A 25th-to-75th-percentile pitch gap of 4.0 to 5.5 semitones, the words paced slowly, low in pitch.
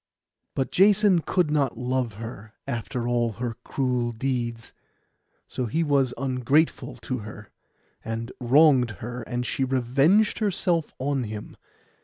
No: average, 3.5 semitones; slow, 130 wpm; low, 125 Hz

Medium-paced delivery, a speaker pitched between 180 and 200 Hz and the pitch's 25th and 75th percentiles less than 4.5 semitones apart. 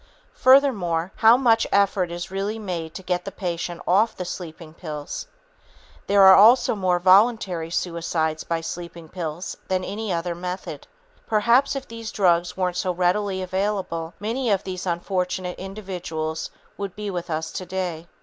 Yes: average, 155 wpm; medium, 185 Hz; average, 3.0 semitones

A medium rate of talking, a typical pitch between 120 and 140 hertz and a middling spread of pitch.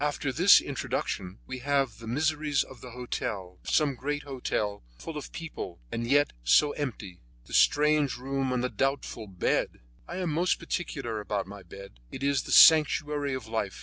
Yes: average, 180 wpm; low, 135 Hz; average, 4.9 semitones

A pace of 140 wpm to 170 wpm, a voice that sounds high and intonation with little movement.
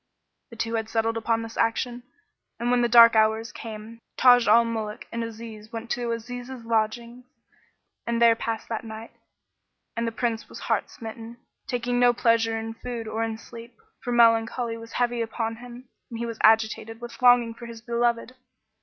No: average, 180 wpm; high, 230 Hz; narrow, 1.0 semitones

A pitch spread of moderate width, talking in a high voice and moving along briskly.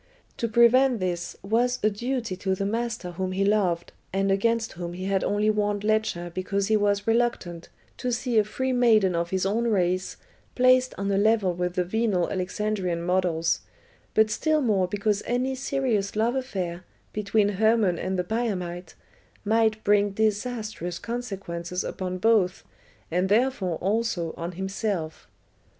No: average, 3.7 semitones; high, 205 Hz; average, 155 wpm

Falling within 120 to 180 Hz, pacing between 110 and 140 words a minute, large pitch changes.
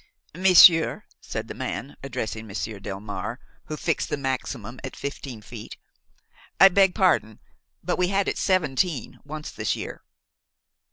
Yes: medium, 140 Hz; slow, 135 wpm; wide, 8.1 semitones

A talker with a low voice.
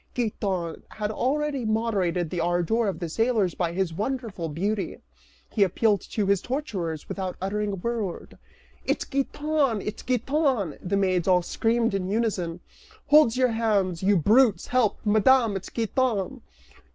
No: high, 210 Hz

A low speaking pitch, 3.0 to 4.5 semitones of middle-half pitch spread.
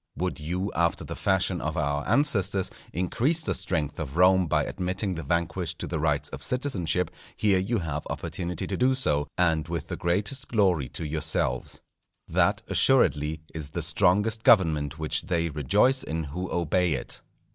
Yes: very low, 85 Hz; average, 3.8 semitones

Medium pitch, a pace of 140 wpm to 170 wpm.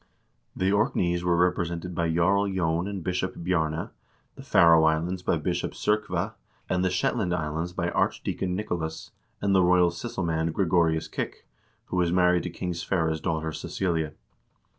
No: very low, 90 Hz; average, 155 wpm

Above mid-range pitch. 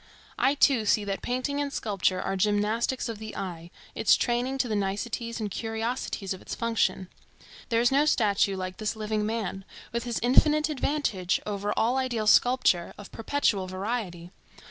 Yes: high, 220 Hz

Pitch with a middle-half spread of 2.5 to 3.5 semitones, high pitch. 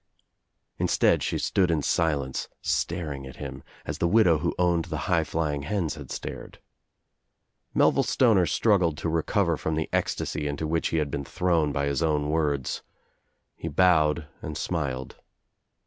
No: average, 2.8 semitones; very low, 80 Hz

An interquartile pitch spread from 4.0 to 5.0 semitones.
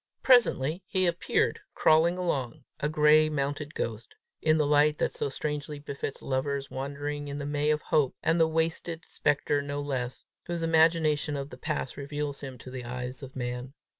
No: narrow, 2.4 semitones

